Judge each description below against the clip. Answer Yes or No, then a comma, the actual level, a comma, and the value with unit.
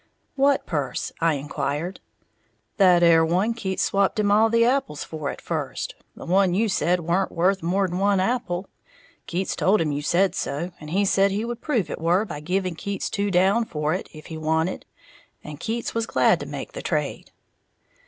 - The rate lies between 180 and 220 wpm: Yes, average, 190 wpm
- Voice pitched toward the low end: No, medium, 185 Hz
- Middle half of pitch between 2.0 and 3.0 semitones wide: No, average, 3.9 semitones